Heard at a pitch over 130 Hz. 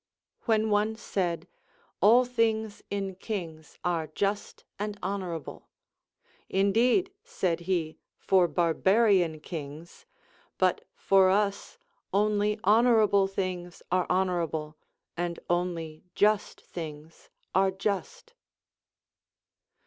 Yes: high, 190 Hz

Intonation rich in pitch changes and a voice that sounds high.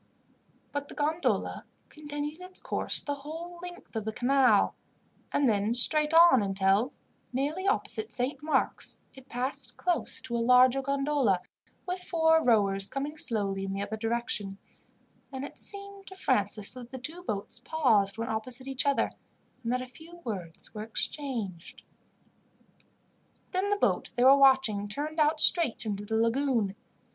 Yes: wide, 5.8 semitones; very high, 260 Hz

